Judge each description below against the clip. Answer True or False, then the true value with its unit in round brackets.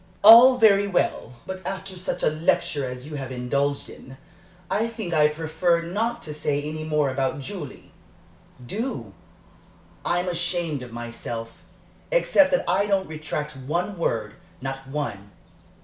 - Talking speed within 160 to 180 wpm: False (145 wpm)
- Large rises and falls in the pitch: True (5.8 semitones)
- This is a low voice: False (155 Hz)